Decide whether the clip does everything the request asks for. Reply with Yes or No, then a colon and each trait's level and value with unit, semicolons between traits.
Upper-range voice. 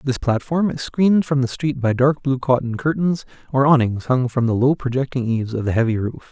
No: low, 130 Hz